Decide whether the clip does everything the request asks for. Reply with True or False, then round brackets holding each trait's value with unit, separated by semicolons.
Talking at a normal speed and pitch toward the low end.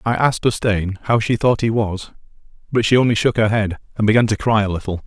False (235 wpm; 110 Hz)